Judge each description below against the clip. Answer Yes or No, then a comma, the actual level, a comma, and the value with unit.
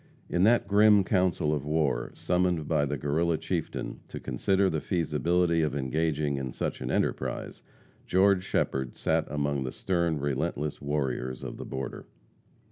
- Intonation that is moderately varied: Yes, average, 3.9 semitones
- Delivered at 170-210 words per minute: No, average, 150 wpm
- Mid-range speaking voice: No, very low, 75 Hz